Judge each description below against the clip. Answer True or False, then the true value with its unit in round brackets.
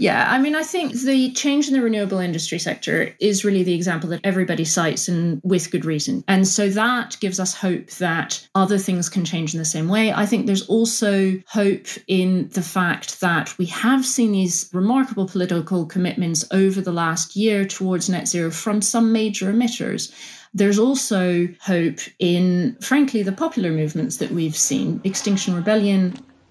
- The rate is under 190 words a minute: True (175 wpm)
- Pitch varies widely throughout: False (3.6 semitones)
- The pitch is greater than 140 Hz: True (190 Hz)